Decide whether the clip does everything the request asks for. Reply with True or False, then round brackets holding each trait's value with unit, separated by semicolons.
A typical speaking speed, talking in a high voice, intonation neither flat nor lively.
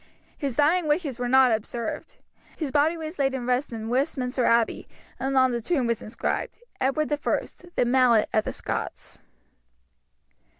True (160 wpm; 260 Hz; 3.5 semitones)